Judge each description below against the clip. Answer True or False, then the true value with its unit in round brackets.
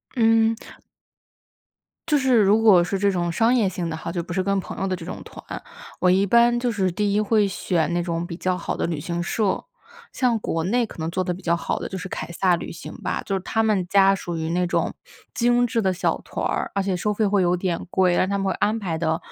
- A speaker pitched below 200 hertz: True (190 Hz)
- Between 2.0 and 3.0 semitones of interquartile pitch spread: False (3.6 semitones)